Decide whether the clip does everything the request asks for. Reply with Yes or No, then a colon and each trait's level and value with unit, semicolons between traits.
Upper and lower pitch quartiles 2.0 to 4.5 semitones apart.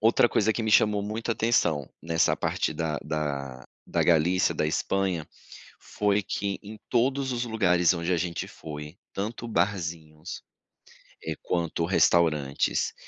No: average, 5.0 semitones